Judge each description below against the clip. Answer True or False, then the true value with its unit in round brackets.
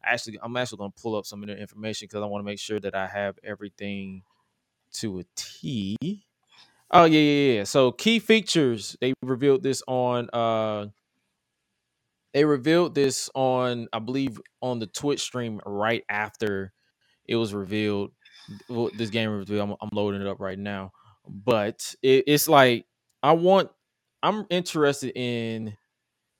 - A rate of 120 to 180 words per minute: True (160 wpm)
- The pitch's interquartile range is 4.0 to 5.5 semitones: True (4.4 semitones)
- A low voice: True (115 Hz)